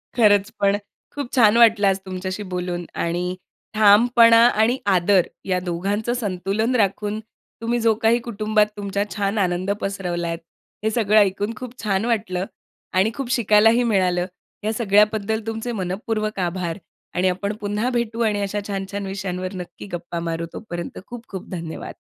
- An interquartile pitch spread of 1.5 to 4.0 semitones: Yes, average, 3.1 semitones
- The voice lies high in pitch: Yes, high, 205 Hz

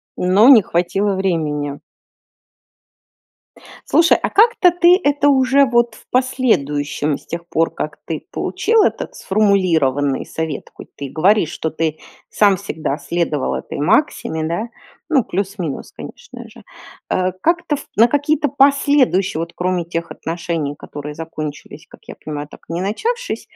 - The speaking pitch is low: No, medium, 185 Hz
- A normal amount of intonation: No, wide, 8.9 semitones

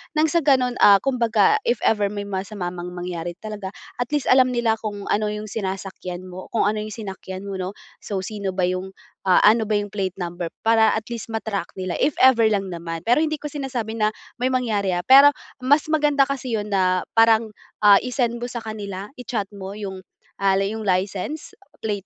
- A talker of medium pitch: No, high, 210 Hz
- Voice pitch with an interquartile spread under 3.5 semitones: No, average, 3.9 semitones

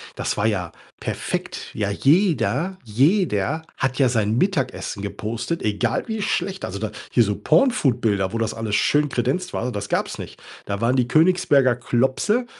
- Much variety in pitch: Yes, wide, 7.1 semitones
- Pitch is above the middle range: No, low, 125 Hz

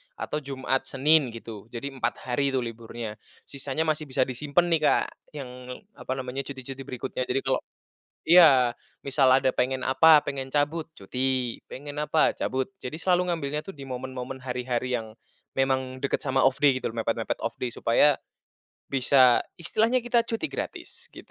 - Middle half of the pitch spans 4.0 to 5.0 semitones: No, average, 2.7 semitones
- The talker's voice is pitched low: Yes, low, 130 Hz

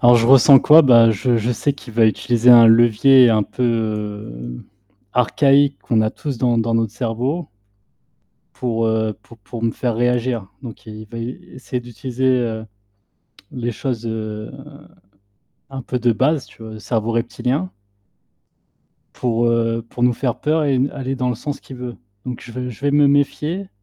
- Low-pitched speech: Yes, low, 120 Hz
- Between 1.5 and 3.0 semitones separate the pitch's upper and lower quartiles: Yes, narrow, 2.5 semitones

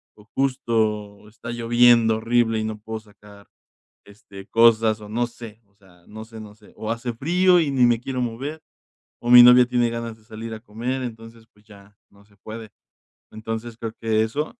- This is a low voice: Yes, low, 115 Hz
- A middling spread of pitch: No, narrow, 1.9 semitones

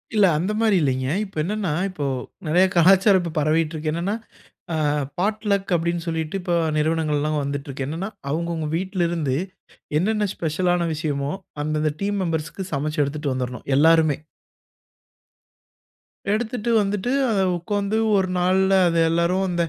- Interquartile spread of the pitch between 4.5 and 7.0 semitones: No, average, 4.0 semitones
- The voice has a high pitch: No, medium, 170 Hz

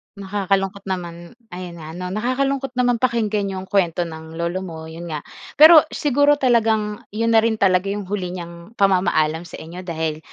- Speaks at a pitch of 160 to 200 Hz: Yes, high, 190 Hz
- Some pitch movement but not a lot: Yes, average, 4.6 semitones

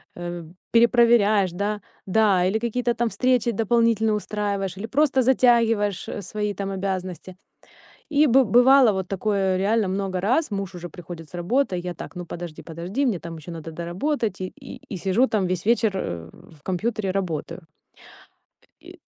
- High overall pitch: Yes, high, 200 Hz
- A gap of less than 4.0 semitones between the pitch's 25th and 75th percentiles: No, average, 4.4 semitones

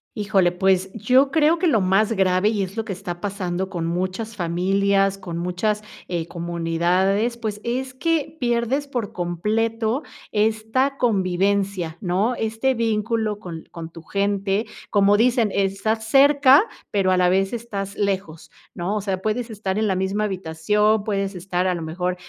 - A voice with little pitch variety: No, average, 3.3 semitones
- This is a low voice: No, high, 200 Hz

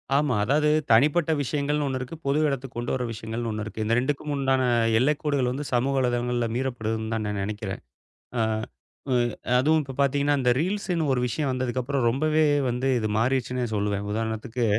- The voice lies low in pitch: Yes, low, 130 Hz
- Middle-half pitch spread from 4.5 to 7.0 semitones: No, average, 3.7 semitones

